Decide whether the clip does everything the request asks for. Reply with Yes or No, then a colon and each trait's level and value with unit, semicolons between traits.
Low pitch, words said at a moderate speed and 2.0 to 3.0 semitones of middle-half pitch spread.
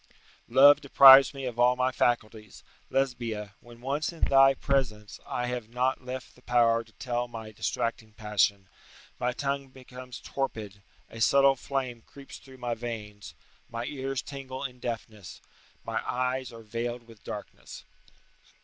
Yes: low, 125 Hz; average, 150 wpm; average, 2.7 semitones